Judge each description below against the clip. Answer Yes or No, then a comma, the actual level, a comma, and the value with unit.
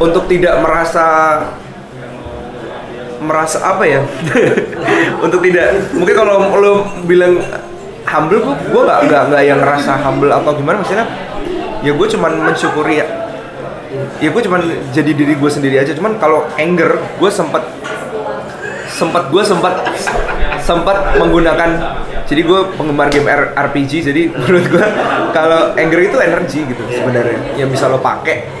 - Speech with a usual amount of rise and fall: Yes, average, 3.7 semitones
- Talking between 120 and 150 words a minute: Yes, average, 135 wpm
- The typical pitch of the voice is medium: Yes, medium, 155 Hz